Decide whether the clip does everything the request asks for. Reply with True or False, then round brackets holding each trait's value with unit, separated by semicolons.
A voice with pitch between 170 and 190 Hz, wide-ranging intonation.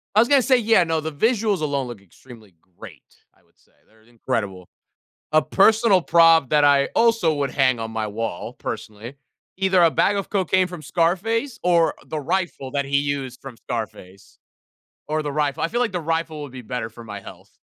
False (150 Hz; 7.1 semitones)